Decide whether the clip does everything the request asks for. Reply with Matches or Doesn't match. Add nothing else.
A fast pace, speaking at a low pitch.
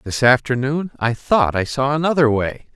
Doesn't match